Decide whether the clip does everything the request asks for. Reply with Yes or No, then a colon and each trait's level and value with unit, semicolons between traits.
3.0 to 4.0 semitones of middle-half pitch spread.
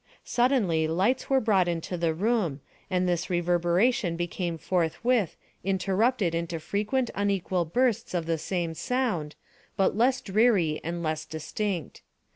No: average, 4.5 semitones